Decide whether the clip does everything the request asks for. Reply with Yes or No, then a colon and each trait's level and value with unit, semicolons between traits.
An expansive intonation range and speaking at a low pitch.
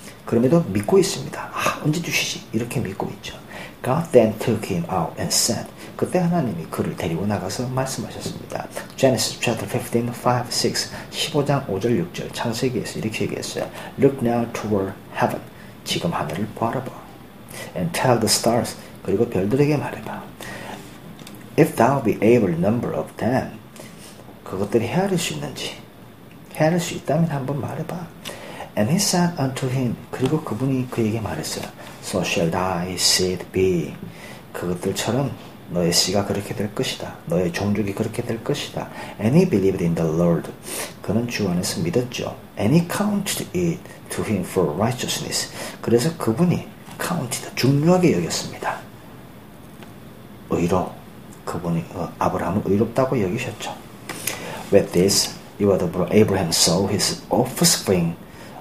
Yes: wide, 8.6 semitones; low, 130 Hz